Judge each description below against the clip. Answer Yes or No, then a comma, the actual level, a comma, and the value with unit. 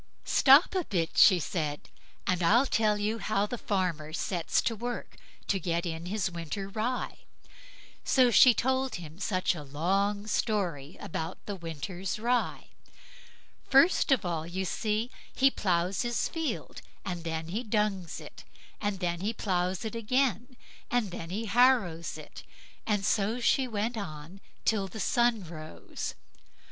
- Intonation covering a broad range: No, average, 4.9 semitones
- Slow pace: No, average, 155 wpm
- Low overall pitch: No, high, 200 Hz